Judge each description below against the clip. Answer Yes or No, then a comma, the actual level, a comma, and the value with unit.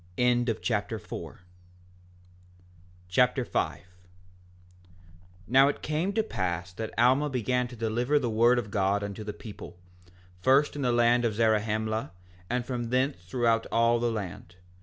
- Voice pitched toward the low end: Yes, low, 120 Hz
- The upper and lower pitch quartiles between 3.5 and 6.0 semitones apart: No, average, 2.8 semitones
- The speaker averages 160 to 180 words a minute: No, average, 140 wpm